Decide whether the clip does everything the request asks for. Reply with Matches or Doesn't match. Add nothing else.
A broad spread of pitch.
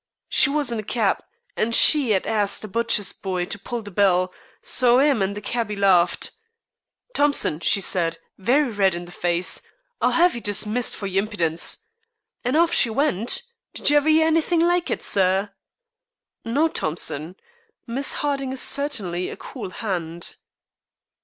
Matches